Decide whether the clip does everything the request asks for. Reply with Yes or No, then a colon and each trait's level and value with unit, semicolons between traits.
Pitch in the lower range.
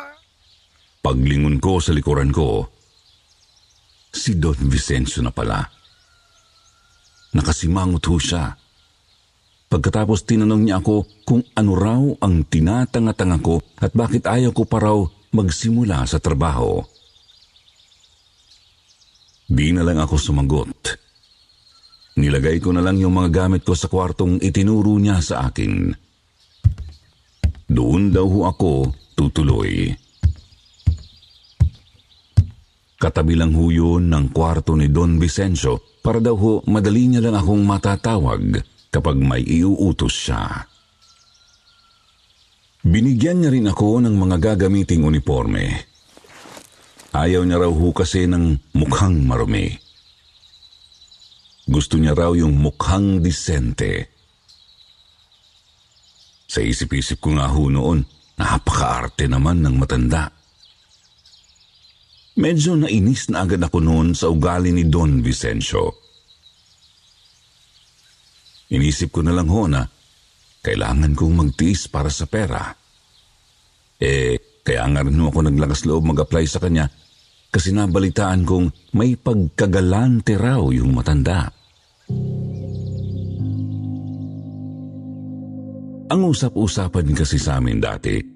Yes: very low, 90 Hz